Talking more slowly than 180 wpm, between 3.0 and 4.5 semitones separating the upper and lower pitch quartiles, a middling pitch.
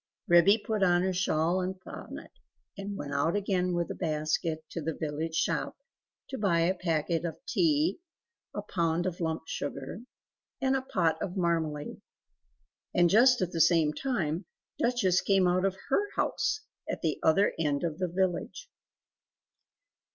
Yes: average, 160 wpm; average, 3.5 semitones; medium, 175 Hz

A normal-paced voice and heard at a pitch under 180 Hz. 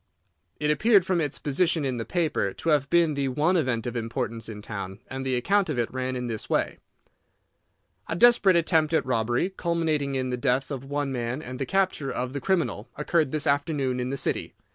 No: fast, 210 wpm; medium, 140 Hz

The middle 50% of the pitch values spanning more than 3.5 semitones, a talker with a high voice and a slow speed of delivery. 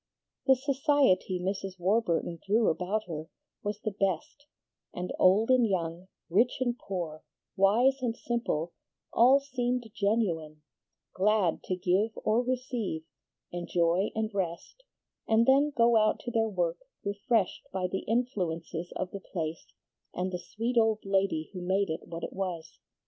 No: average, 4.8 semitones; high, 195 Hz; average, 145 wpm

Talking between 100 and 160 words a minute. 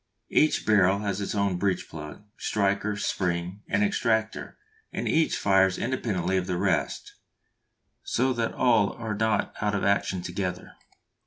Yes: average, 145 wpm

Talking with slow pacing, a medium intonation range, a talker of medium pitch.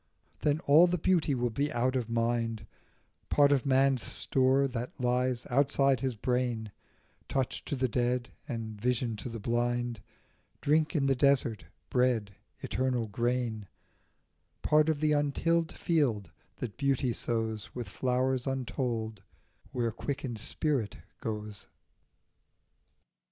No: slow, 125 wpm; average, 3.0 semitones; low, 125 Hz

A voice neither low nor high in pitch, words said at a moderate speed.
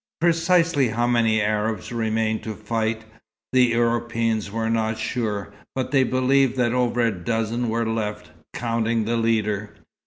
No: low, 115 Hz; average, 145 wpm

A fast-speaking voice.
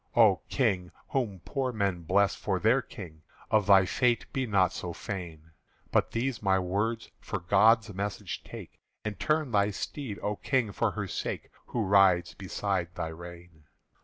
No: average, 160 wpm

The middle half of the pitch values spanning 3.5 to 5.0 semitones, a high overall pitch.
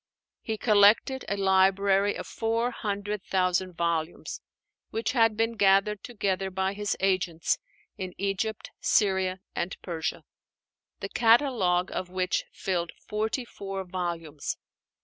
No: narrow, 2.6 semitones; high, 195 Hz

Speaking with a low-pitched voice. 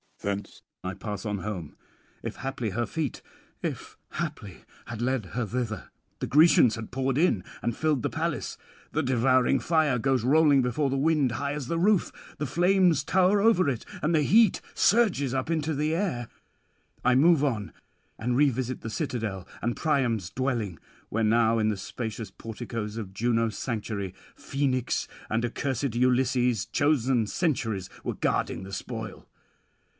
Yes: low, 125 Hz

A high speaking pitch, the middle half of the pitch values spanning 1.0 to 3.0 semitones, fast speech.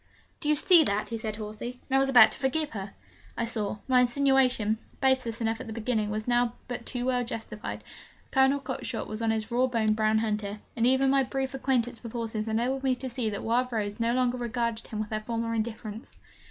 Yes: high, 235 Hz; average, 2.7 semitones; fast, 220 wpm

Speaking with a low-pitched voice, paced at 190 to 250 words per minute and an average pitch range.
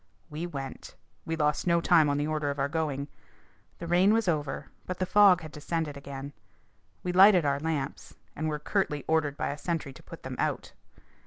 No: medium, 155 Hz; average, 195 wpm; average, 3.3 semitones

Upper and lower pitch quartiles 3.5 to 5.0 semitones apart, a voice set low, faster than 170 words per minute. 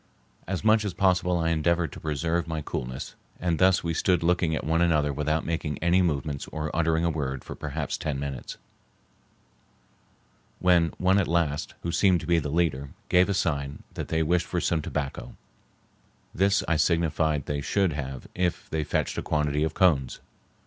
No: average, 2.8 semitones; very low, 80 Hz; average, 180 wpm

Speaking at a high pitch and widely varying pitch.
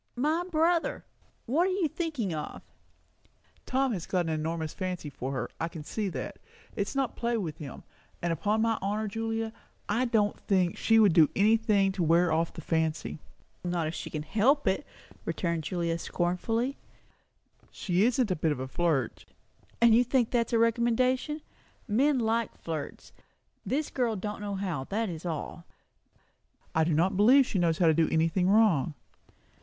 Yes: high, 200 Hz; wide, 5.9 semitones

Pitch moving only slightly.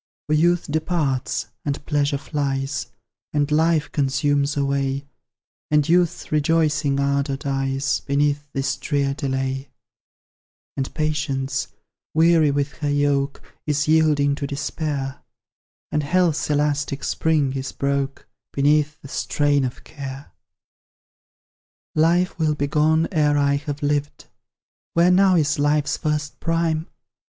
Yes: narrow, 1.7 semitones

